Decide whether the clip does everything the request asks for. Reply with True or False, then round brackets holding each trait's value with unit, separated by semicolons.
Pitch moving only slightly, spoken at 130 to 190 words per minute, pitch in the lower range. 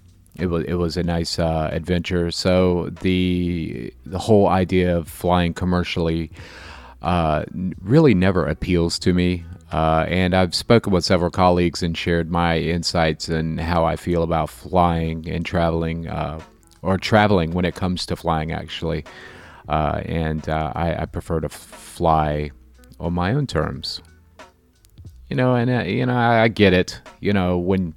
True (2.0 semitones; 165 wpm; 85 Hz)